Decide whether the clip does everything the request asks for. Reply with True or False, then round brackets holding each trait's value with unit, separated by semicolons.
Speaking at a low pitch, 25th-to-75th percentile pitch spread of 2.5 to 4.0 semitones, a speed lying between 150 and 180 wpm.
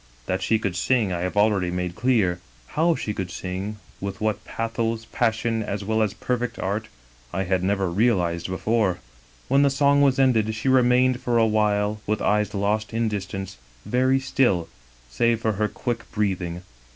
True (110 Hz; 3.6 semitones; 175 wpm)